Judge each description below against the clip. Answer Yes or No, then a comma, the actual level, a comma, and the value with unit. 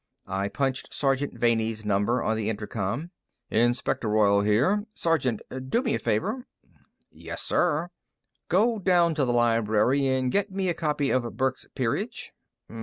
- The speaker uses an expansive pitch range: Yes, wide, 6.9 semitones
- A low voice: Yes, low, 130 Hz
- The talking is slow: No, average, 145 wpm